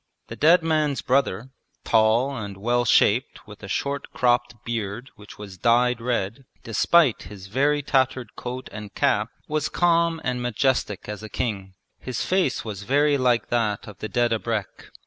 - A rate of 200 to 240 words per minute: No, average, 165 wpm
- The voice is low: Yes, low, 120 Hz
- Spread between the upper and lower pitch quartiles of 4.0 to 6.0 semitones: Yes, average, 4.4 semitones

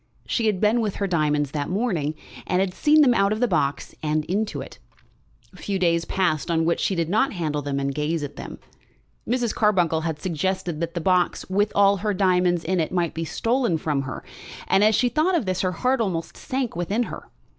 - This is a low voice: No, medium, 185 Hz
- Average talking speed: No, fast, 215 wpm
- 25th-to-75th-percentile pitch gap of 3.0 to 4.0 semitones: No, average, 4.6 semitones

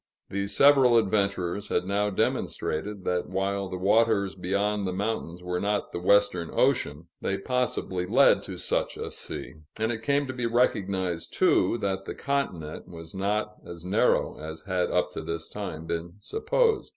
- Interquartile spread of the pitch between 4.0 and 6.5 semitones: No, average, 3.3 semitones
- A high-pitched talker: No, low, 100 Hz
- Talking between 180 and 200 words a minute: No, average, 165 wpm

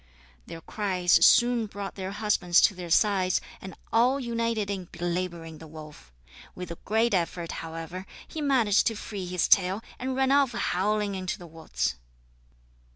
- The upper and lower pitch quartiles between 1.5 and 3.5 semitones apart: No, average, 4.3 semitones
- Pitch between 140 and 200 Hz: Yes, high, 190 Hz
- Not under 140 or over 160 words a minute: Yes, average, 155 wpm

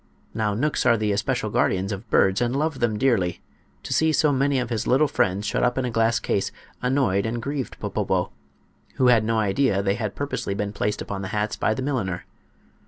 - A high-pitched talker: No, low, 115 Hz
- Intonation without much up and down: No, average, 4.3 semitones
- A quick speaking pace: Yes, fast, 210 wpm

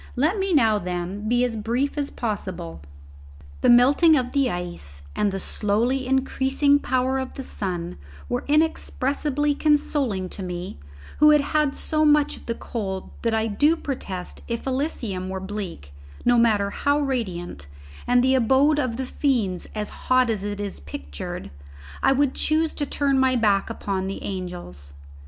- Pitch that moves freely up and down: Yes, wide, 6.4 semitones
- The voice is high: Yes, high, 240 Hz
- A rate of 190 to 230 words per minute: No, average, 165 wpm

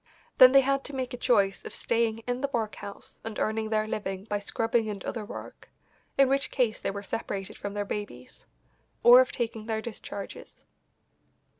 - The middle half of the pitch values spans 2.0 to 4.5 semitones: Yes, average, 3.3 semitones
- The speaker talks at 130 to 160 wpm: No, average, 180 wpm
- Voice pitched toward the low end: No, high, 220 Hz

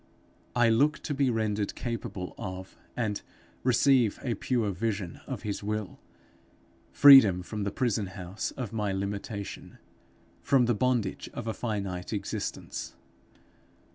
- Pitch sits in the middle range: No, low, 105 Hz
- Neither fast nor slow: No, slow, 130 wpm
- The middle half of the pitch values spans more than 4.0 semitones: No, average, 3.4 semitones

